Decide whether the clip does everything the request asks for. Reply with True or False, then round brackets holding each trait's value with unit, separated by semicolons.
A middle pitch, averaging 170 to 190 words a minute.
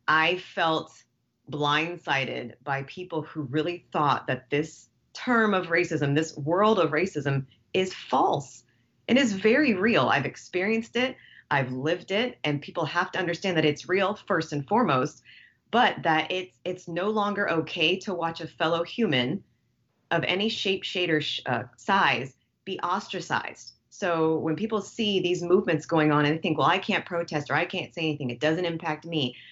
True (170 Hz; 175 wpm)